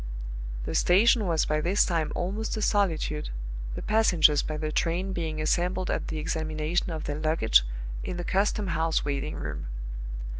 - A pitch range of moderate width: Yes, average, 3.4 semitones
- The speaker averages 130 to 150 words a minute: No, average, 160 wpm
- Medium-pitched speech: Yes, medium, 165 Hz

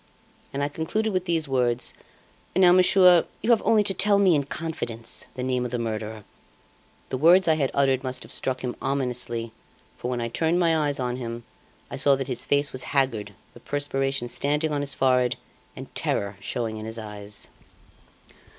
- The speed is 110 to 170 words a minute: No, average, 185 wpm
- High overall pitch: No, low, 135 Hz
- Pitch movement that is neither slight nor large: Yes, average, 4.9 semitones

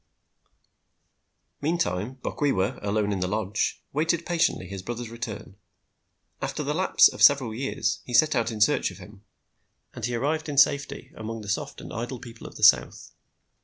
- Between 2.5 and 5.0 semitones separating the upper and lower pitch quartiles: No, wide, 5.4 semitones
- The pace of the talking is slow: No, average, 165 wpm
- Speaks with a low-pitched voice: Yes, low, 115 Hz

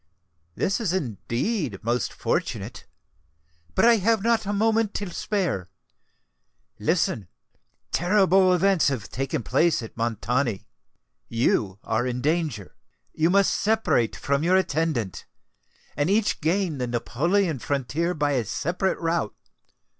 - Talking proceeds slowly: Yes, slow, 125 wpm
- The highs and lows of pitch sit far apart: Yes, wide, 8.1 semitones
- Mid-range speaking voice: Yes, medium, 160 Hz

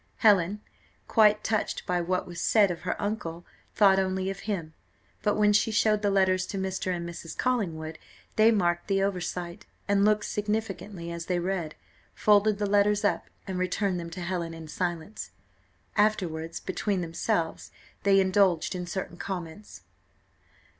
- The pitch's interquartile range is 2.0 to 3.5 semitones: Yes, average, 3.2 semitones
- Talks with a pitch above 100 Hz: Yes, high, 190 Hz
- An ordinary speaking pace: Yes, average, 155 wpm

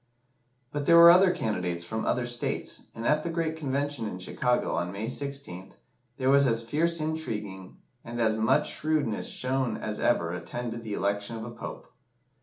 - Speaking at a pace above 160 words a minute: Yes, average, 175 wpm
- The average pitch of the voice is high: No, low, 120 Hz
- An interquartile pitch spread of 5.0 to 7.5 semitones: Yes, wide, 5.4 semitones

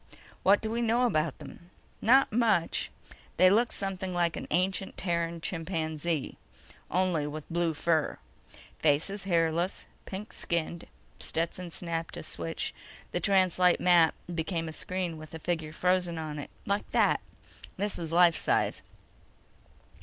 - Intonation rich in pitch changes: No, average, 2.7 semitones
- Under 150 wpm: Yes, average, 140 wpm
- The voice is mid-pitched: Yes, medium, 175 Hz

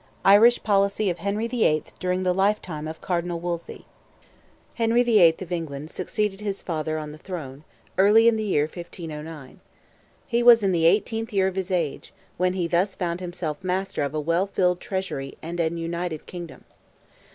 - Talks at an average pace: Yes, average, 180 wpm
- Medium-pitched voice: Yes, medium, 180 Hz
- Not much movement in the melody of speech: No, average, 3.3 semitones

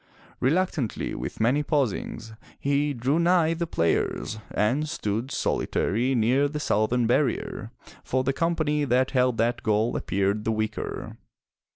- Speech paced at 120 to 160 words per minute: Yes, slow, 135 wpm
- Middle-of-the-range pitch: No, low, 130 Hz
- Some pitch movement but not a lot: Yes, average, 4.9 semitones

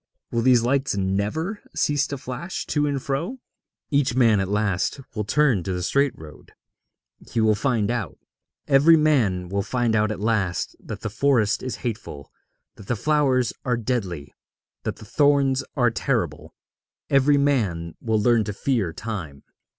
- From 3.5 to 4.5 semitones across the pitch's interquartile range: No, average, 5.3 semitones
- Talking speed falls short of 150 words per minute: No, average, 160 wpm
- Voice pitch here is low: Yes, low, 115 Hz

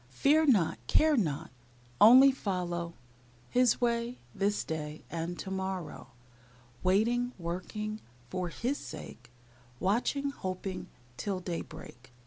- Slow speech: Yes, slow, 110 wpm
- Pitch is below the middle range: No, high, 190 Hz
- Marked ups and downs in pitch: Yes, wide, 5.9 semitones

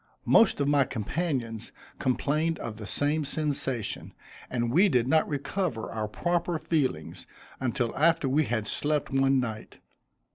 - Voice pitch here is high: No, low, 135 Hz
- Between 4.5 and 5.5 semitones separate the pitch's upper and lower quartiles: Yes, average, 4.9 semitones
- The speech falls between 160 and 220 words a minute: No, average, 140 wpm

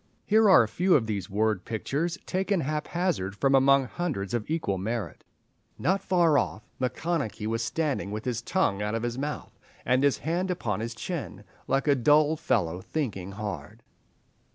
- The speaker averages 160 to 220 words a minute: Yes, average, 170 wpm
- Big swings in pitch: Yes, wide, 7.0 semitones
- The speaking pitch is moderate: No, low, 130 Hz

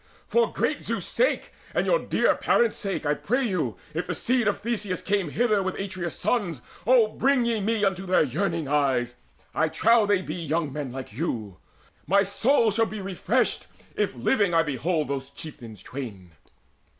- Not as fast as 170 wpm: No, average, 175 wpm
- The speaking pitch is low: No, medium, 185 Hz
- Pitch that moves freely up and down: Yes, wide, 6.9 semitones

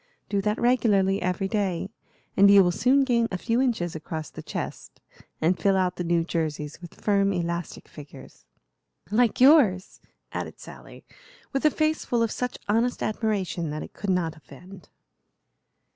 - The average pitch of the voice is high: Yes, high, 195 Hz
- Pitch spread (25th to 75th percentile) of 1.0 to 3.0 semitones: No, average, 5.0 semitones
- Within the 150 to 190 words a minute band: Yes, average, 160 wpm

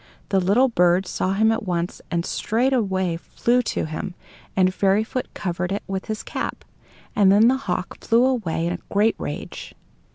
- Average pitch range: Yes, average, 4.0 semitones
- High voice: Yes, high, 195 Hz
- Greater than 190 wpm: No, average, 170 wpm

